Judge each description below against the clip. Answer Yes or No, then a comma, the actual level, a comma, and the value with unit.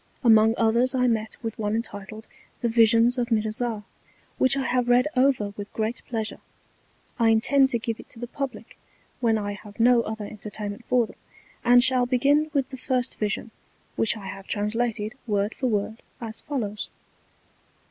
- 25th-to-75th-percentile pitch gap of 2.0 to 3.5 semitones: Yes, narrow, 2.5 semitones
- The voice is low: No, high, 230 Hz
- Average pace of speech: Yes, average, 170 wpm